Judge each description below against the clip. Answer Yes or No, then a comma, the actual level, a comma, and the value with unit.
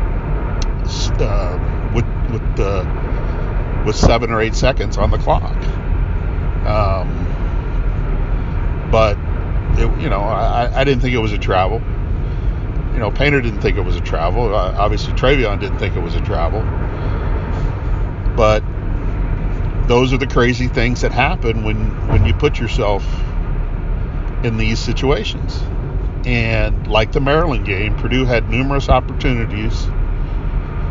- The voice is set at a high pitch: No, low, 105 Hz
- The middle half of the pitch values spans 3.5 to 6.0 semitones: Yes, average, 4.4 semitones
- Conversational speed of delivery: No, slow, 130 wpm